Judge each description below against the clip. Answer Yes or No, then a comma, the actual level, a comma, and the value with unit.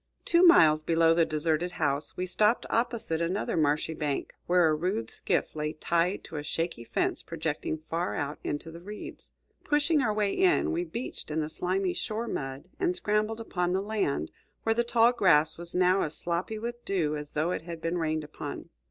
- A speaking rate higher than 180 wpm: Yes, average, 195 wpm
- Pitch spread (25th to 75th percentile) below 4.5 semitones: No, wide, 5.5 semitones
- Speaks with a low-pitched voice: No, medium, 175 Hz